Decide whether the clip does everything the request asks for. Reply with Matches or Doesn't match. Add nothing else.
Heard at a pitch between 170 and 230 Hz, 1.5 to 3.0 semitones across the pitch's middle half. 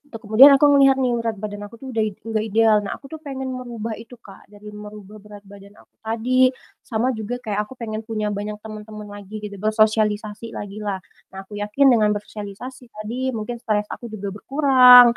Matches